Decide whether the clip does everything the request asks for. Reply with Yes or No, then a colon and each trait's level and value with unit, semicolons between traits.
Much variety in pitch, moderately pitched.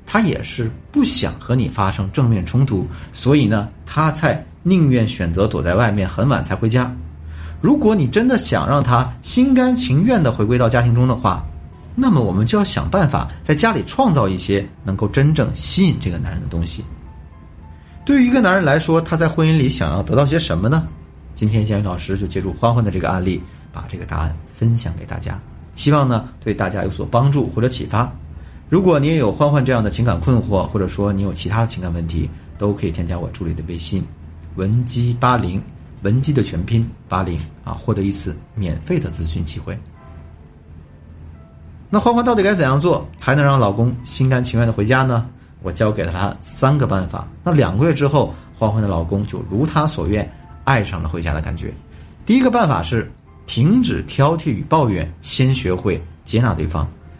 No: wide, 8.2 semitones; low, 105 Hz